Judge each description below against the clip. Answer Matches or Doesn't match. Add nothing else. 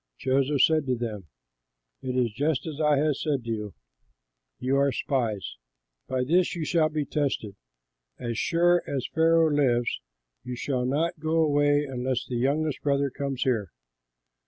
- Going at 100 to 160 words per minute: Matches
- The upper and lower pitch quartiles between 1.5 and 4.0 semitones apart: Matches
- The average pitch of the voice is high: Doesn't match